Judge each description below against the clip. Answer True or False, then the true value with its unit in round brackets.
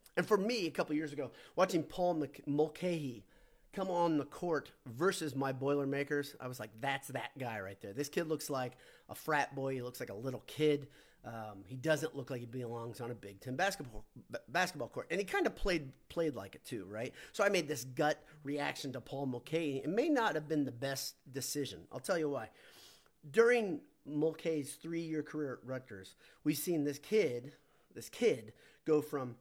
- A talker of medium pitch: True (145 Hz)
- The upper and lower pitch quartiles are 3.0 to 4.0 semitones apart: True (3.4 semitones)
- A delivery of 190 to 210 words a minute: True (200 wpm)